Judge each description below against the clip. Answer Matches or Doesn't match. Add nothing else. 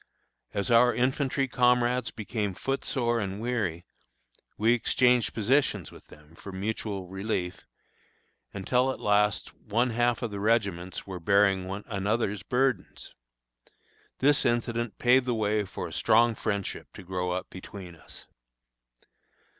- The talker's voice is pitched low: Matches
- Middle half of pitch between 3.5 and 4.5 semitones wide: Matches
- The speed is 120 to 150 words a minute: Matches